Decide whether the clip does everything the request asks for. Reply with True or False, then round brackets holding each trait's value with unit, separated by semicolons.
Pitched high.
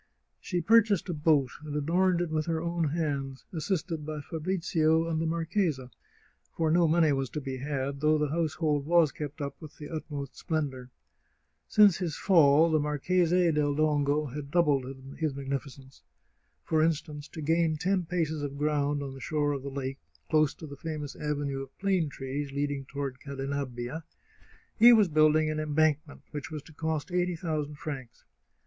False (150 Hz)